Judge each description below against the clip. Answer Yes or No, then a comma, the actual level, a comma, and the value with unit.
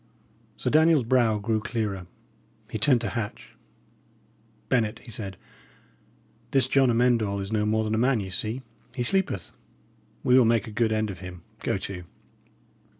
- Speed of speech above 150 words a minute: Yes, average, 165 wpm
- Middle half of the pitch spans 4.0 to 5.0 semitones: No, average, 3.0 semitones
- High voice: No, low, 110 Hz